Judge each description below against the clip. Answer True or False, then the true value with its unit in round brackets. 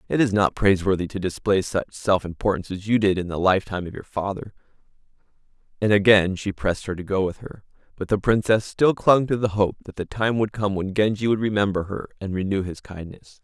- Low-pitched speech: True (100 Hz)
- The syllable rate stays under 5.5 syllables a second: False (6.0 syllables/s)